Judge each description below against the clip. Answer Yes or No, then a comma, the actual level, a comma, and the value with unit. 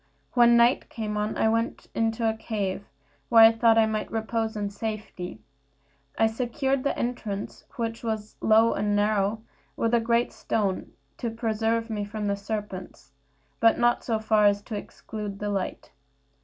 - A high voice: Yes, high, 220 Hz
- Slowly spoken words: No, average, 165 wpm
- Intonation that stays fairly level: Yes, narrow, 1.6 semitones